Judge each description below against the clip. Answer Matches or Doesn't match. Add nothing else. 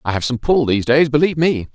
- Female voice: Doesn't match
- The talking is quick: Matches